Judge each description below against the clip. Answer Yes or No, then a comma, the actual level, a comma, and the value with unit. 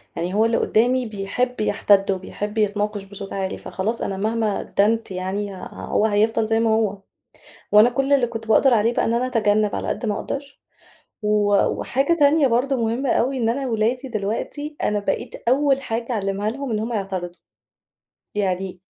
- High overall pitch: Yes, high, 220 Hz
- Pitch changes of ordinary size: Yes, average, 3.3 semitones